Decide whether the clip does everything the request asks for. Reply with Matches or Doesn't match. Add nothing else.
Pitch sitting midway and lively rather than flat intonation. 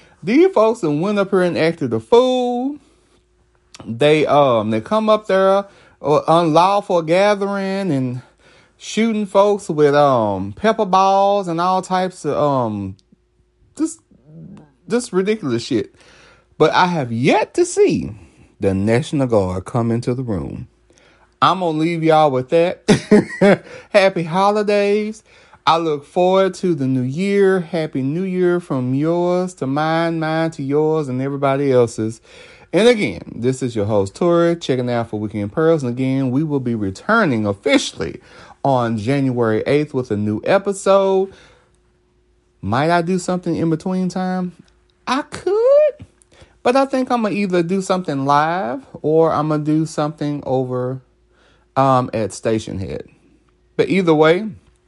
Matches